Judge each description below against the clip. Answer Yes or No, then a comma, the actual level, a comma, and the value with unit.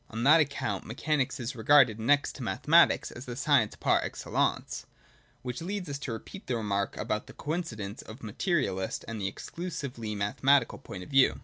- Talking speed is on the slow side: No, average, 190 wpm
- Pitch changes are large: No, average, 4.9 semitones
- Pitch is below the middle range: Yes, low, 125 Hz